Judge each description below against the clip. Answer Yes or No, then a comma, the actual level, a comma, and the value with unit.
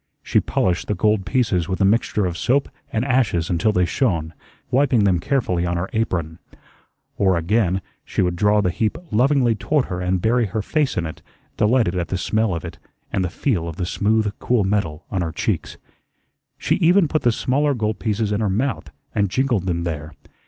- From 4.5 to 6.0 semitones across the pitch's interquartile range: Yes, average, 5.0 semitones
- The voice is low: Yes, low, 100 Hz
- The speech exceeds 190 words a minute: Yes, average, 200 wpm